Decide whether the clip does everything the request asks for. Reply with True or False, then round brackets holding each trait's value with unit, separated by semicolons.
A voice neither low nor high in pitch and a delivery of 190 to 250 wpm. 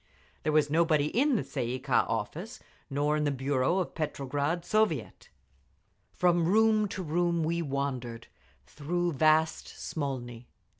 False (155 Hz; 145 wpm)